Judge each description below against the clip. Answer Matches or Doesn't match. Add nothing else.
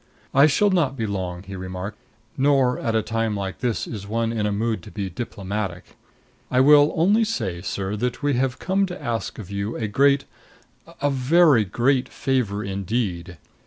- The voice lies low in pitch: Matches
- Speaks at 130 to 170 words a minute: Doesn't match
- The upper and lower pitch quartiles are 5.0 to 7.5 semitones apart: Matches